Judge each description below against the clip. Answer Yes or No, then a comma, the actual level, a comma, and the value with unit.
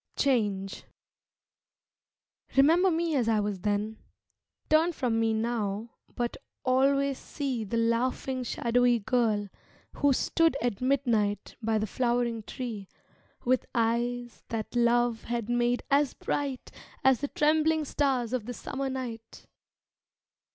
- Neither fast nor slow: No, slow, 125 wpm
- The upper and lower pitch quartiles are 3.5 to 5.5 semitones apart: No, average, 3.0 semitones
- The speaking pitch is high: Yes, high, 240 Hz